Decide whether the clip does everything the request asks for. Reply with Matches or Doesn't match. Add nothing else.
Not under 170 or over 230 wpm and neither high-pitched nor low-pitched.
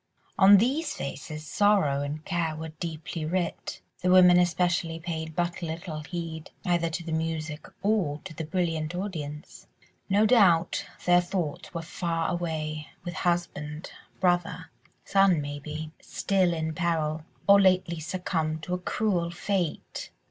Doesn't match